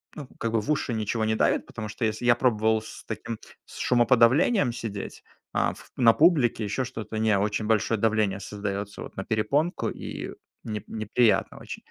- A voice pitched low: Yes, low, 110 Hz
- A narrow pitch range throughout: Yes, narrow, 2.2 semitones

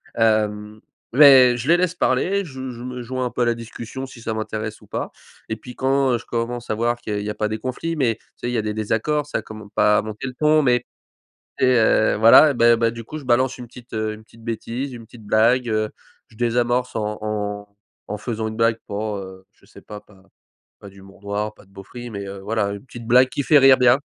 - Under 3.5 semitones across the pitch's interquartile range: Yes, average, 2.9 semitones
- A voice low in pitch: Yes, low, 115 Hz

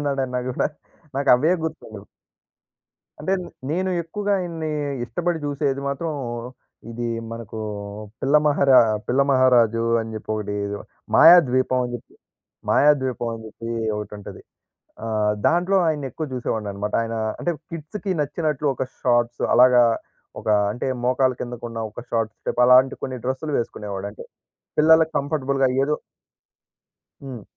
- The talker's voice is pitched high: No, low, 130 Hz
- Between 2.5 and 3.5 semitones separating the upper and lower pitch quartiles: No, average, 4.4 semitones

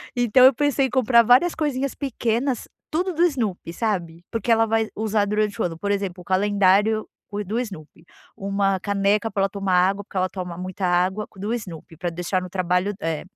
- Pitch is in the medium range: No, high, 205 Hz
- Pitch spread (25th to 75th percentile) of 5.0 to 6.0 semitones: No, average, 3.9 semitones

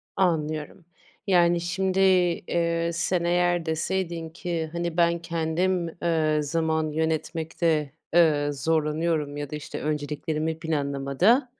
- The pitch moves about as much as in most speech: No, narrow, 2.0 semitones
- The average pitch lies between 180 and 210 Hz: No, medium, 165 Hz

